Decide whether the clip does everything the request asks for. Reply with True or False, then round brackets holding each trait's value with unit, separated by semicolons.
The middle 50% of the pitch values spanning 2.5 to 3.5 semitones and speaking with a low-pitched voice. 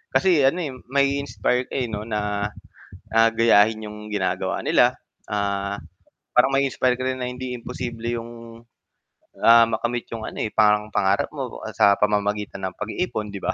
True (3.1 semitones; 115 Hz)